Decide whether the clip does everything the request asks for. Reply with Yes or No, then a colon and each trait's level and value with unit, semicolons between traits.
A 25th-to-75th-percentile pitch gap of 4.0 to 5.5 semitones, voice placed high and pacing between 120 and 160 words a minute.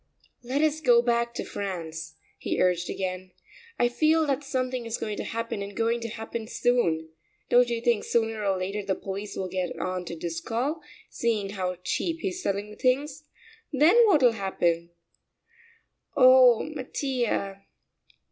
Yes: average, 5.0 semitones; high, 230 Hz; average, 155 wpm